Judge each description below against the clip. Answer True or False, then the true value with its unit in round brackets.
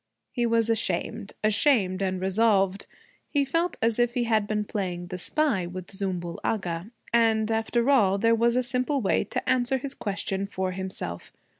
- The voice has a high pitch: True (215 Hz)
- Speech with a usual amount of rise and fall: True (4.0 semitones)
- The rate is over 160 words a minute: True (170 wpm)